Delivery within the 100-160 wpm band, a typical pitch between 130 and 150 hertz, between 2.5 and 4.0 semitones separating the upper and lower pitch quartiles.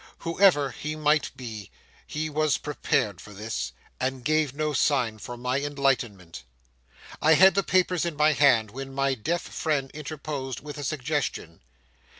Yes: average, 155 wpm; medium, 140 Hz; average, 3.7 semitones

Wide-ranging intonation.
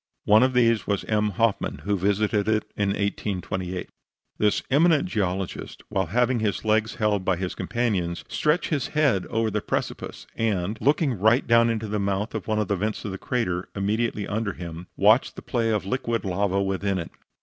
No: average, 2.9 semitones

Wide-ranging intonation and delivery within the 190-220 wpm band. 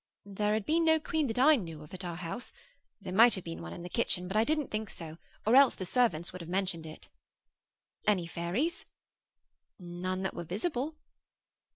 Yes: wide, 6.0 semitones; average, 195 wpm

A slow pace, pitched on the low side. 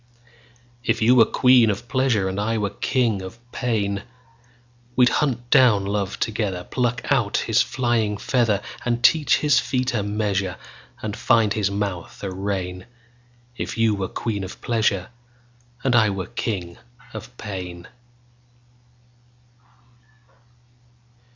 Yes: slow, 110 wpm; low, 115 Hz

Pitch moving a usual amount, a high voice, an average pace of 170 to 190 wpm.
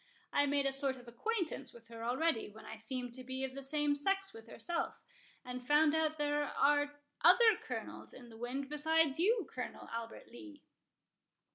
Yes: average, 4.0 semitones; very high, 280 Hz; average, 180 wpm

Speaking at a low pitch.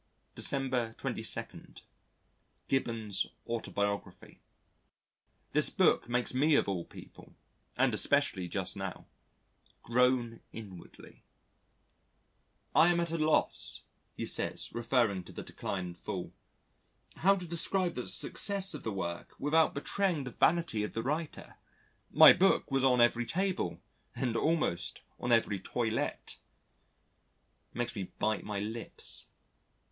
Yes: low, 120 Hz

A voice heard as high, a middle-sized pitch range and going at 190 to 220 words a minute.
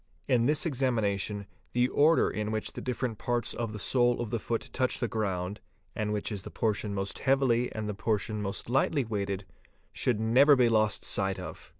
No: low, 110 Hz; average, 3.1 semitones; average, 195 wpm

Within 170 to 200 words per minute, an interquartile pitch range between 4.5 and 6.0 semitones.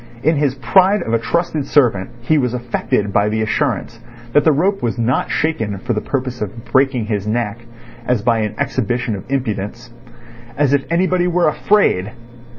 Yes: average, 175 wpm; average, 5.2 semitones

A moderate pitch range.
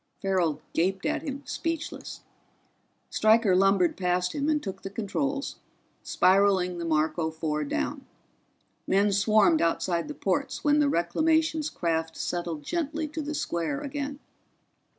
No: wide, 9.0 semitones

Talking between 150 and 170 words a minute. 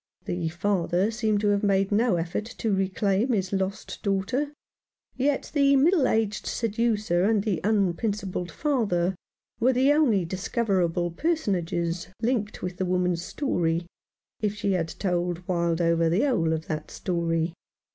No: average, 140 wpm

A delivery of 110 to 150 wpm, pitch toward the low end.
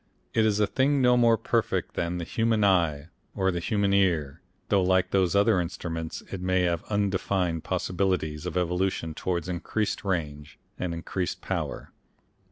No: average, 160 wpm; very low, 90 Hz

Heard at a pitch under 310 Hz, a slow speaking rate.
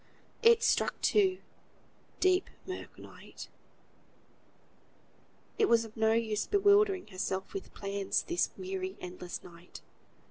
No: very high, 350 Hz; slow, 110 wpm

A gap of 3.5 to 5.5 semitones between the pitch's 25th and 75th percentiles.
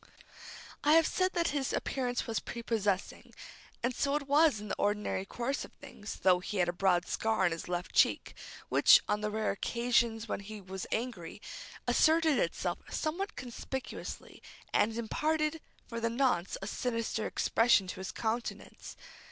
Yes: average, 5.2 semitones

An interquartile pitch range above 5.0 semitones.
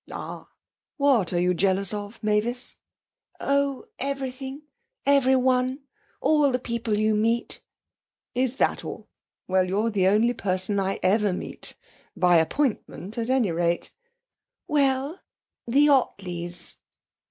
Yes: wide, 5.6 semitones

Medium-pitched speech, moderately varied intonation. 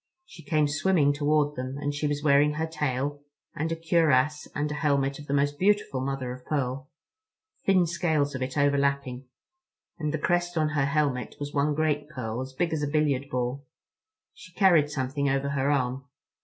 No: medium, 145 Hz; narrow, 2.0 semitones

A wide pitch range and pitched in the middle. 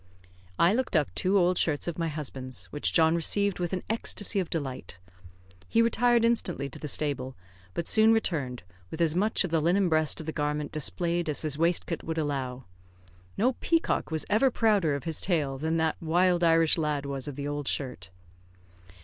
No: average, 4.0 semitones; medium, 160 Hz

